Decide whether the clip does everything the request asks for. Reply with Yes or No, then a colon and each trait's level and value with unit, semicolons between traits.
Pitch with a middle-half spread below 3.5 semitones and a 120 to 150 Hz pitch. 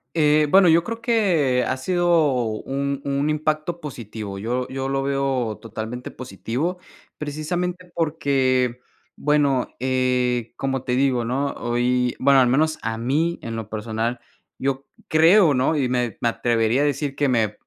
No: average, 3.8 semitones; low, 135 Hz